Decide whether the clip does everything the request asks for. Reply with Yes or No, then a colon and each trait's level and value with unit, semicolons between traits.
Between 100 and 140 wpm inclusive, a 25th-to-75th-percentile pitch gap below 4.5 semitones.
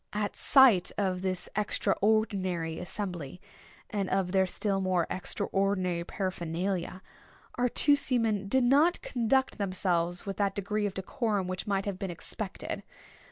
Yes: slow, 135 wpm; narrow, 2.6 semitones